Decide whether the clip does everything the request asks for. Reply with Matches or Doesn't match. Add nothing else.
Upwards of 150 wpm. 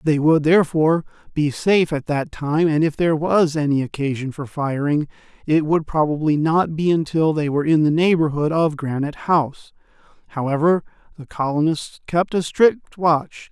Matches